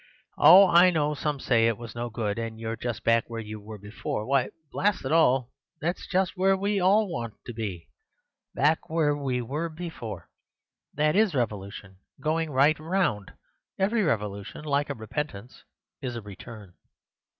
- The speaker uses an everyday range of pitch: No, wide, 6.5 semitones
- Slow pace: No, average, 160 wpm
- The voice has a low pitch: Yes, low, 130 Hz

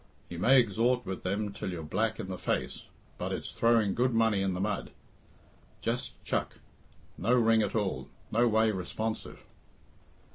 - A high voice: No, low, 110 Hz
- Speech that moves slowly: No, average, 160 wpm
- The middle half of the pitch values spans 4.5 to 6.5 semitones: No, average, 3.2 semitones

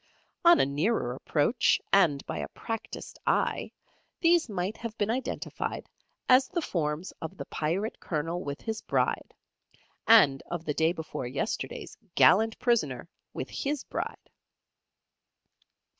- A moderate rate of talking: No, slow, 130 wpm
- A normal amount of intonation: No, wide, 7.4 semitones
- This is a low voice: No, high, 190 Hz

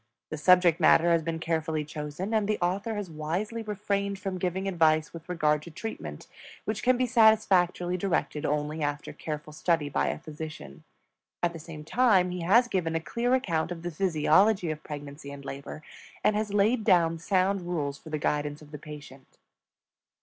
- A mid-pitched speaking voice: Yes, medium, 170 Hz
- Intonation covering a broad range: No, average, 4.4 semitones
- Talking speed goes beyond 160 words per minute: Yes, average, 180 wpm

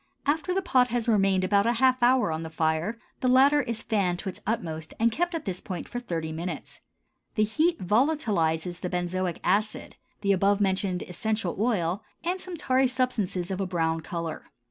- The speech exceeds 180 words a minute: Yes, average, 190 wpm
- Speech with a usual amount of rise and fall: No, wide, 6.0 semitones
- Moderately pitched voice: No, high, 200 Hz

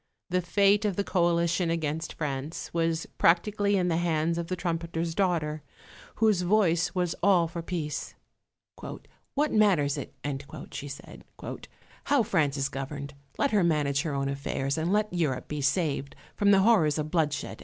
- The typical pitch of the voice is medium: Yes, medium, 170 Hz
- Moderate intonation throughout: Yes, average, 3.8 semitones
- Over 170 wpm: No, average, 160 wpm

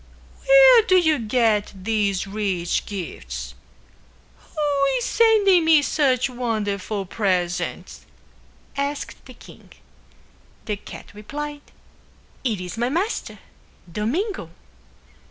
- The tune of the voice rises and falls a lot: Yes, wide, 7.0 semitones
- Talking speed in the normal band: No, slow, 100 wpm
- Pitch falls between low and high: No, high, 230 Hz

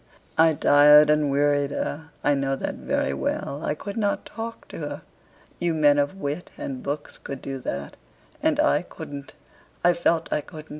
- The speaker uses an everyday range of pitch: No, narrow, 2.3 semitones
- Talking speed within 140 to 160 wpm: No, average, 180 wpm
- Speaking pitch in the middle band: Yes, medium, 145 Hz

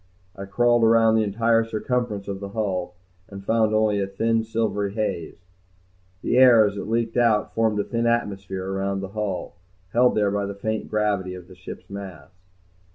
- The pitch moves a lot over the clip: No, narrow, 2.5 semitones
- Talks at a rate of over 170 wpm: Yes, average, 180 wpm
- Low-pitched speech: Yes, low, 105 Hz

